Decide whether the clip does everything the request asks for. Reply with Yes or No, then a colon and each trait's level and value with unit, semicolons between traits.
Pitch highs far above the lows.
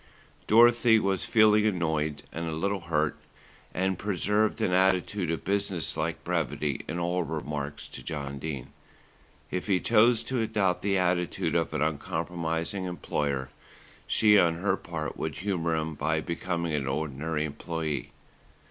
No: average, 4.0 semitones